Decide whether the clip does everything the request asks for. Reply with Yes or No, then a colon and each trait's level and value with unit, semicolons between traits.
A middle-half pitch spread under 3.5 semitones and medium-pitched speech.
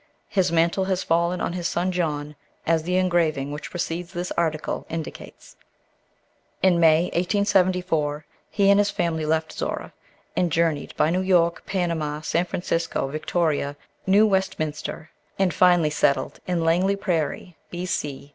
Yes: narrow, 2.6 semitones; medium, 170 Hz